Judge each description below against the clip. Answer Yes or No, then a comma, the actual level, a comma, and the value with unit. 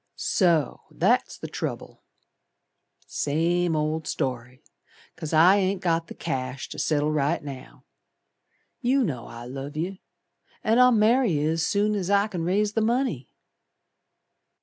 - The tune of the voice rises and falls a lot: Yes, wide, 5.7 semitones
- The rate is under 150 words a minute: Yes, average, 140 wpm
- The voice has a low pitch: No, medium, 165 Hz